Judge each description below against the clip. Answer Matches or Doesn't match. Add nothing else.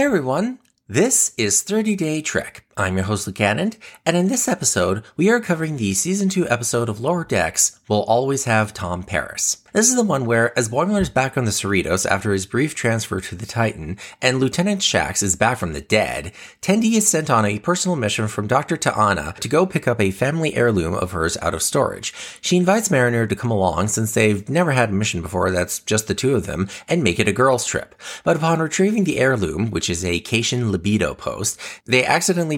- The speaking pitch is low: Matches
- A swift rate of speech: Matches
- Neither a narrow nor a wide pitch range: Doesn't match